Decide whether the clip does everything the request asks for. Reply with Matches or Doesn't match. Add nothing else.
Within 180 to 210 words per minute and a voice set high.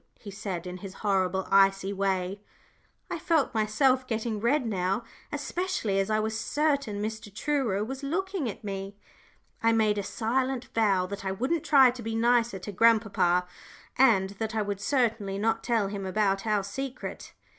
Doesn't match